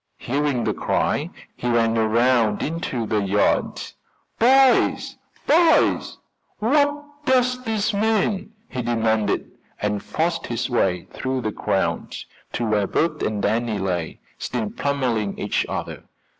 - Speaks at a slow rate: Yes, slow, 125 wpm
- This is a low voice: Yes, low, 120 Hz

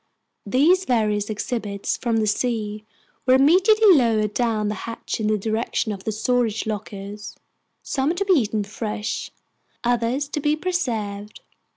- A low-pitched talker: No, high, 225 Hz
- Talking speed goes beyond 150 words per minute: No, average, 145 wpm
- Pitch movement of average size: Yes, average, 4.0 semitones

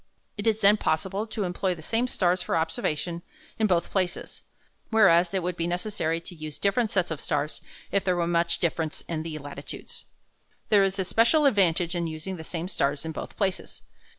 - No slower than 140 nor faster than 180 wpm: No, average, 195 wpm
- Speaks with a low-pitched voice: No, medium, 175 Hz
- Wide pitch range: No, average, 3.5 semitones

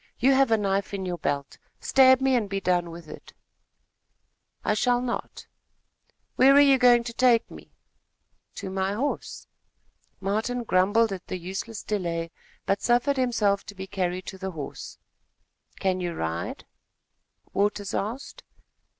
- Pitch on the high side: Yes, high, 200 Hz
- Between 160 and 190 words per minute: No, average, 150 wpm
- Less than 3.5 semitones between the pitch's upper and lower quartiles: No, average, 4.7 semitones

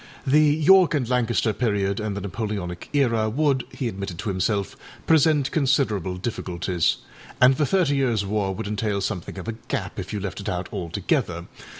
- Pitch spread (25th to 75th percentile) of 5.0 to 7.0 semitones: Yes, wide, 5.6 semitones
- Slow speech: No, average, 175 wpm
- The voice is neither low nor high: No, low, 110 Hz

